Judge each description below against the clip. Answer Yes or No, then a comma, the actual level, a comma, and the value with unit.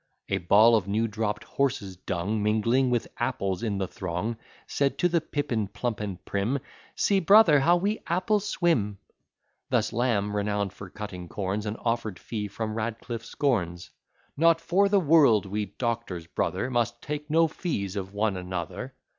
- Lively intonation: Yes, wide, 5.8 semitones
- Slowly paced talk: No, average, 165 wpm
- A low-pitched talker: Yes, low, 110 Hz